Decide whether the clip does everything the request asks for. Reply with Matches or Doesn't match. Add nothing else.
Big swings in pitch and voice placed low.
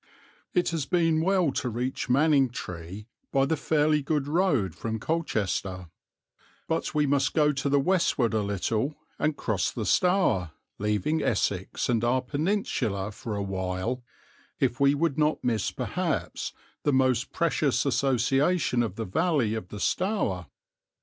Matches